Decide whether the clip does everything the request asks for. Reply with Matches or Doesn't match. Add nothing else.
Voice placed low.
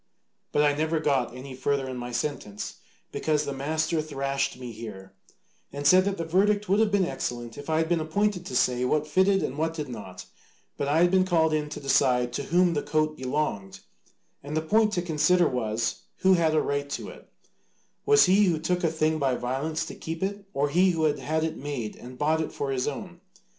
Doesn't match